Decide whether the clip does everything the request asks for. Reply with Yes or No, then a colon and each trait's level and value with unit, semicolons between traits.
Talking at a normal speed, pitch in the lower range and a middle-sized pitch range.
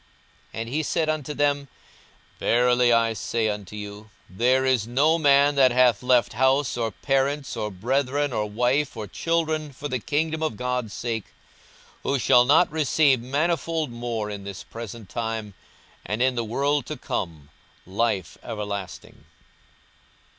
Yes: average, 155 wpm; low, 125 Hz; average, 4.3 semitones